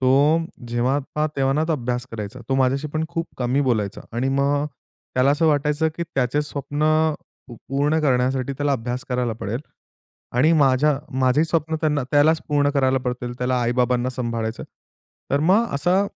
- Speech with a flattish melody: No, average, 3.0 semitones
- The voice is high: No, low, 135 Hz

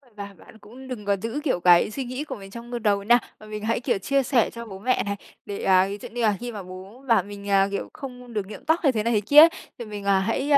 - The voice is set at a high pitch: Yes, high, 215 Hz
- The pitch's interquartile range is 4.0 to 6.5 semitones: No, average, 3.6 semitones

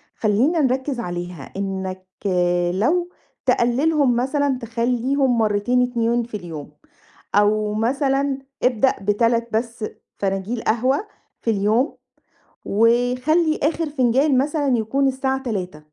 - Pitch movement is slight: No, average, 4.1 semitones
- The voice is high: Yes, high, 240 Hz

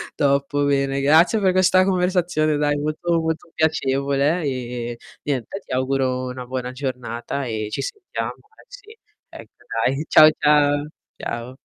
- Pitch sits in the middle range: Yes, medium, 145 Hz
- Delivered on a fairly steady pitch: No, average, 4.3 semitones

